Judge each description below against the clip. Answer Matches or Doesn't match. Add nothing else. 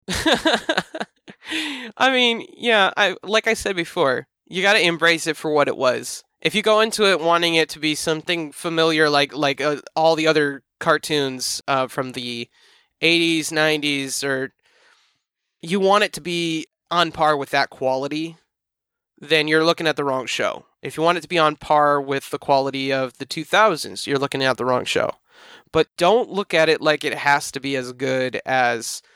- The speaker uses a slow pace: Doesn't match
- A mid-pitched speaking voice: Matches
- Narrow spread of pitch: Doesn't match